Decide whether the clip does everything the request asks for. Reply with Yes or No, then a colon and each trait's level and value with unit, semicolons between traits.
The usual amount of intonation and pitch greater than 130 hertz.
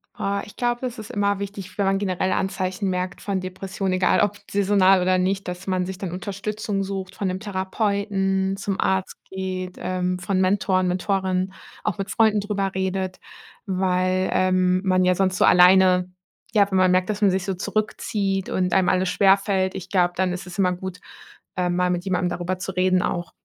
No: narrow, 1.3 semitones; high, 190 Hz